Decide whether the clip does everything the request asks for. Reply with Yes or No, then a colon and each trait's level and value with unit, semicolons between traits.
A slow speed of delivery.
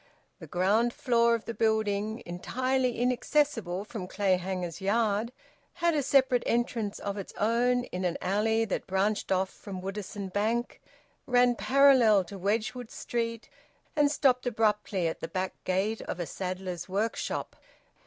No: average, 145 wpm